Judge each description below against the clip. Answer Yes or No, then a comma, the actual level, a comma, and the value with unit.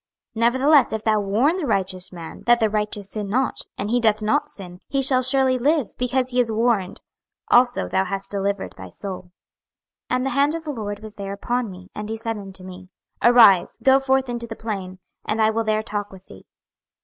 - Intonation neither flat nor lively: Yes, average, 4.1 semitones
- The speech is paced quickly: Yes, fast, 215 wpm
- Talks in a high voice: Yes, high, 220 Hz